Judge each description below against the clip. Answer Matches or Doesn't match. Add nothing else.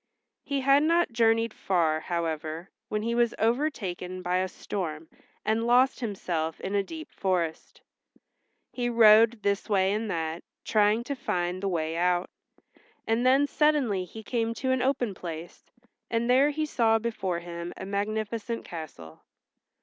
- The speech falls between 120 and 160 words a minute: Matches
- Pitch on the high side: Matches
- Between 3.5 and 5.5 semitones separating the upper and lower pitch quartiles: Matches